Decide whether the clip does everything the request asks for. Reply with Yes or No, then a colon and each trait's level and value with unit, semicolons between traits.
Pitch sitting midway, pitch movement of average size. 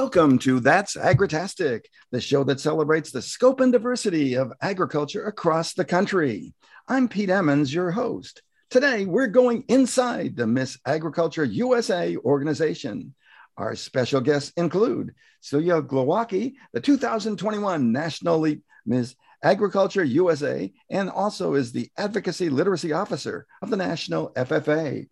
No: medium, 175 Hz; wide, 7.2 semitones